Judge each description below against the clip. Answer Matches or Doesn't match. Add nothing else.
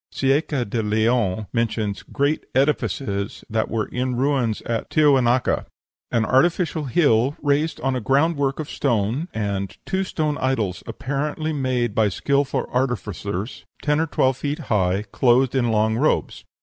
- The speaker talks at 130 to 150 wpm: Matches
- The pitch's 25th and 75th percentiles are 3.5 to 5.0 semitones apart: Matches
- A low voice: Matches